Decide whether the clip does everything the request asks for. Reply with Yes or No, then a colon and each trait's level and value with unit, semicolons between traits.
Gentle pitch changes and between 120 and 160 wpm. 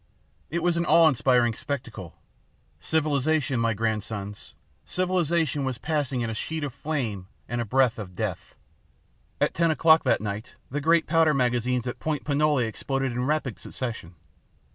No: average, 5.1 semitones; average, 155 wpm